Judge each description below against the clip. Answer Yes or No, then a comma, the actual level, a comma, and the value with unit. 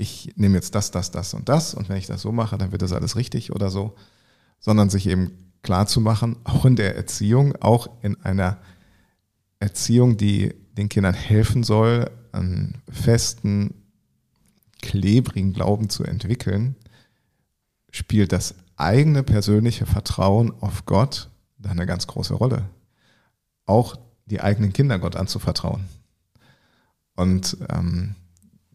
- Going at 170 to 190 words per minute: No, average, 130 wpm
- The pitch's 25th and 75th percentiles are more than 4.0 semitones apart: No, average, 3.4 semitones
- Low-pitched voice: Yes, low, 105 Hz